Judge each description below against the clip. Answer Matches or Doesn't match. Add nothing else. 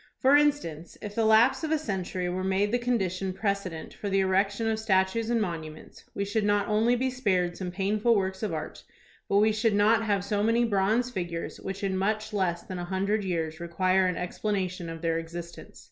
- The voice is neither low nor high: Doesn't match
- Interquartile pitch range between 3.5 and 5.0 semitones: Doesn't match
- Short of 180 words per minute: Doesn't match